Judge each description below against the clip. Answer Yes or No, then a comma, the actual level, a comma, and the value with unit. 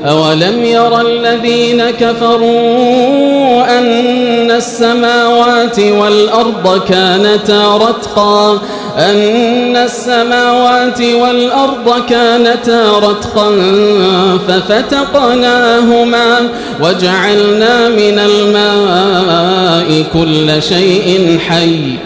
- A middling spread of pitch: Yes, average, 3.1 semitones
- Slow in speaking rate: Yes, slow, 55 wpm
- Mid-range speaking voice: No, high, 230 Hz